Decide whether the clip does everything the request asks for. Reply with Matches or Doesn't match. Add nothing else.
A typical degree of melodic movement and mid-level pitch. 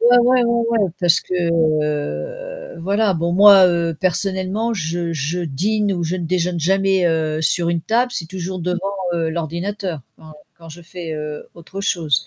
Matches